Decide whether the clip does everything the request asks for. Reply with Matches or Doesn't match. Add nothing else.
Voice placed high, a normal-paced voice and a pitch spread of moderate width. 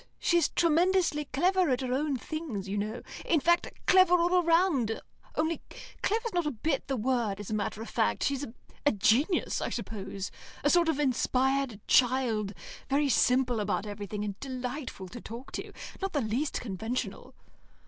Doesn't match